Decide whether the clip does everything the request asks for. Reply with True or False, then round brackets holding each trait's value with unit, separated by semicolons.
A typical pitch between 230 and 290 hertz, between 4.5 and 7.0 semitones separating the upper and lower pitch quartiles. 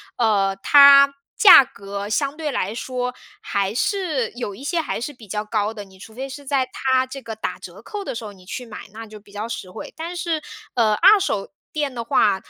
True (240 Hz; 5.1 semitones)